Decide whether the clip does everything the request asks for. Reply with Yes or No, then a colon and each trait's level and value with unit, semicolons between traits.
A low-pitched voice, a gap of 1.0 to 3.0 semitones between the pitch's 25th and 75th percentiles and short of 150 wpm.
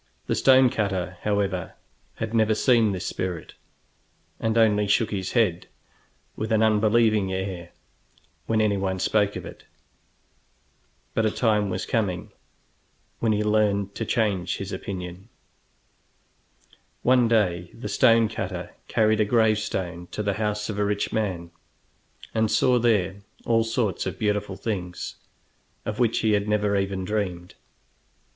Yes: low, 105 Hz; narrow, 2.6 semitones; average, 140 wpm